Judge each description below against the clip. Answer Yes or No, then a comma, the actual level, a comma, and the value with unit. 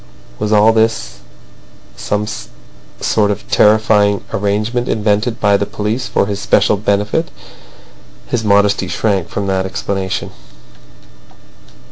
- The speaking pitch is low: Yes, low, 105 Hz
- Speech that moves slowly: Yes, slow, 115 wpm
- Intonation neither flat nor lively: No, narrow, 1.3 semitones